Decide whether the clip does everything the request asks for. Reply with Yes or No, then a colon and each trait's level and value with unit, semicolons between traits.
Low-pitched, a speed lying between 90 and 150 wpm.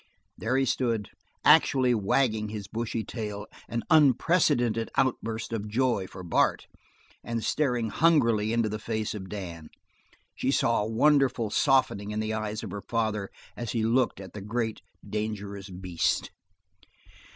Yes: low, 110 Hz; average, 145 wpm